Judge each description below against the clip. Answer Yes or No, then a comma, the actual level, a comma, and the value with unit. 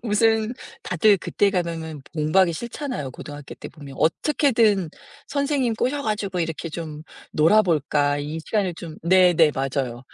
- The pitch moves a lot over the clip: Yes, wide, 6.0 semitones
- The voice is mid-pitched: Yes, medium, 175 Hz